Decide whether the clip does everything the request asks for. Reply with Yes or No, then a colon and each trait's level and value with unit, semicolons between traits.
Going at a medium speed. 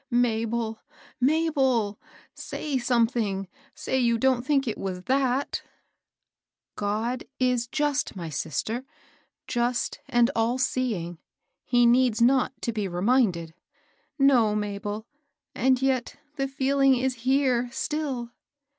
No: slow, 120 wpm